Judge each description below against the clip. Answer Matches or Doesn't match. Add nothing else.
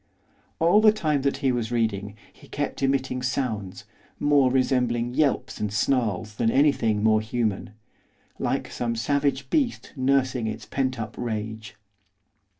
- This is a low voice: Matches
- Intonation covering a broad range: Doesn't match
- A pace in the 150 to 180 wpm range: Doesn't match